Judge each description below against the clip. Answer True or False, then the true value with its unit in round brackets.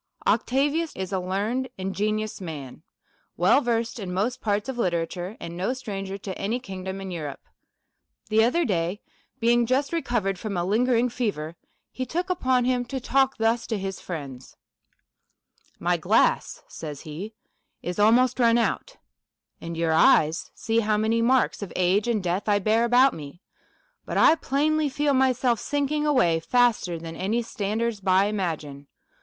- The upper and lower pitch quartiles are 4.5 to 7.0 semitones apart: True (5.2 semitones)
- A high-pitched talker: True (215 Hz)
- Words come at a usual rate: True (165 wpm)